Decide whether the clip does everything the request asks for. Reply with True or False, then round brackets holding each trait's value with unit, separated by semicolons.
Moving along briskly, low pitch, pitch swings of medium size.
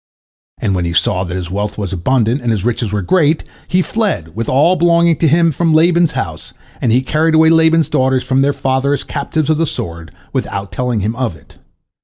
False (215 wpm; 130 Hz; 7.6 semitones)